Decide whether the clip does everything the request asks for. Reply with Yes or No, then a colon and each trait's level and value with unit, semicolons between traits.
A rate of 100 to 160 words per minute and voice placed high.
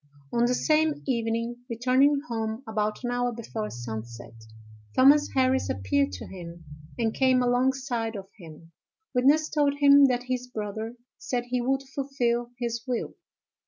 Yes: average, 145 wpm; high, 245 Hz